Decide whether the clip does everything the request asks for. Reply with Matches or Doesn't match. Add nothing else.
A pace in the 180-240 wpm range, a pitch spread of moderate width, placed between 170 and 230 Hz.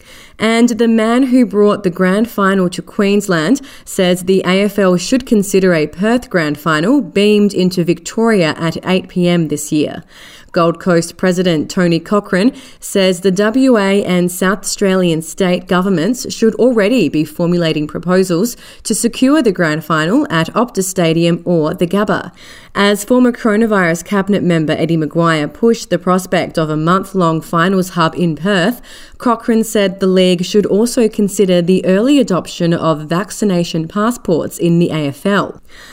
Doesn't match